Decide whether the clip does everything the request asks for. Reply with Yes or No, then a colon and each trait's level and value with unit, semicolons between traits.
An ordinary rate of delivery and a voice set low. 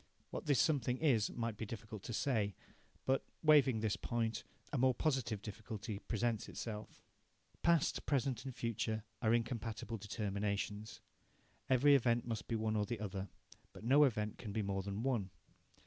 Yes: average, 160 wpm; low, 115 Hz